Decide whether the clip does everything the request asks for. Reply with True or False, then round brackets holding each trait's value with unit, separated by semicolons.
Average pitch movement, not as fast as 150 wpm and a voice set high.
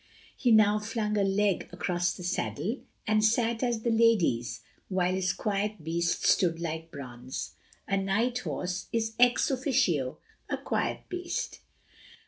True (4.8 semitones; 140 wpm; 200 Hz)